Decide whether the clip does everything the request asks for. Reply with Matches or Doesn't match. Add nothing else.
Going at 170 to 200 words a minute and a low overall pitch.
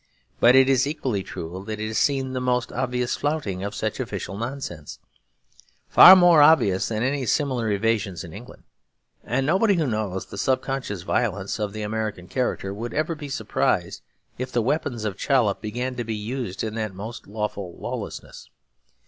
Matches